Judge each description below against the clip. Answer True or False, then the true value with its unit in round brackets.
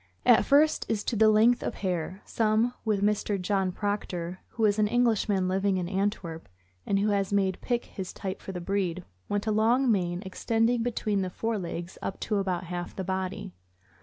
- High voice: True (200 Hz)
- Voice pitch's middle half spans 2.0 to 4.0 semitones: True (2.9 semitones)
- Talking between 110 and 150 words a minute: False (190 wpm)